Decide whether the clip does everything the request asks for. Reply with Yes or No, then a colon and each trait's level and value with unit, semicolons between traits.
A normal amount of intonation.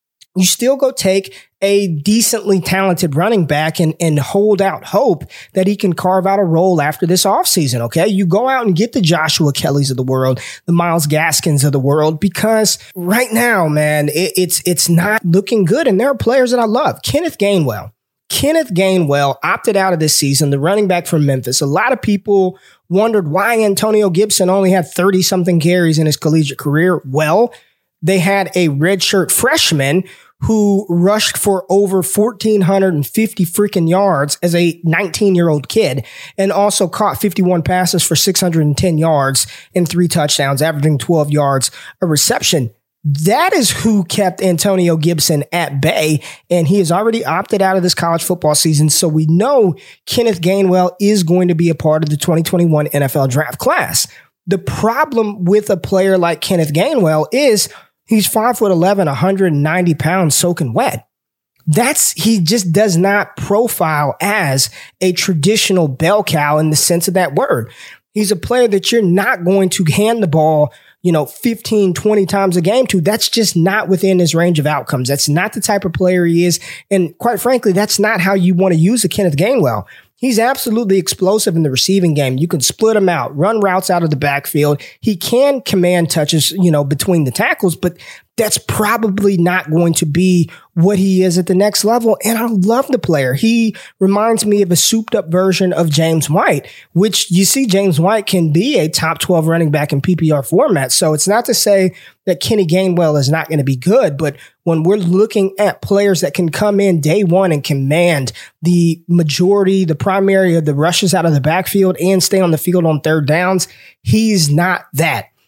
Yes: average, 3.9 semitones